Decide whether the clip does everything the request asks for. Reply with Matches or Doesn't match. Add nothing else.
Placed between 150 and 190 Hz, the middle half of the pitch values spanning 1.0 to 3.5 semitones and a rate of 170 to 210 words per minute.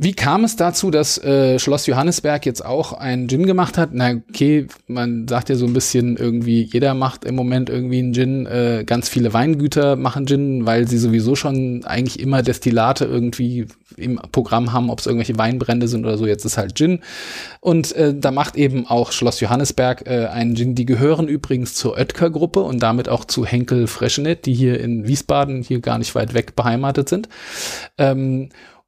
Doesn't match